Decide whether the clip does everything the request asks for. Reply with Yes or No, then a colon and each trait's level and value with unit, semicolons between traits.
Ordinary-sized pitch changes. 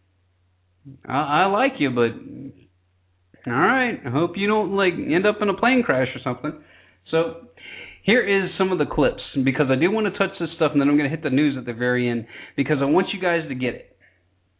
No: wide, 7.5 semitones